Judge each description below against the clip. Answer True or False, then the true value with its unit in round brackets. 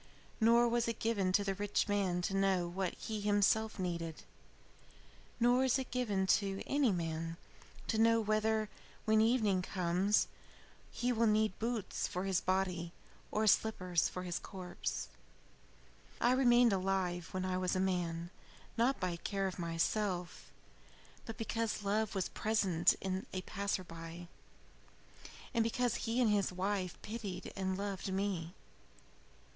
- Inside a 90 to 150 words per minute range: True (145 wpm)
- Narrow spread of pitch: False (3.3 semitones)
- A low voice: False (195 Hz)